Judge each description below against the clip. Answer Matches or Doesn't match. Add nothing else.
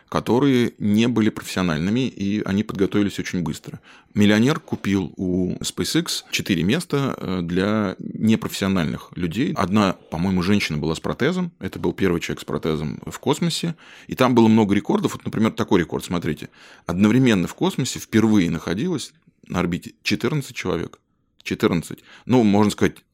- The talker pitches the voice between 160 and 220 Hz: Doesn't match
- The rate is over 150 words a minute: Doesn't match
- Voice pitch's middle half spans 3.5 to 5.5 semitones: Matches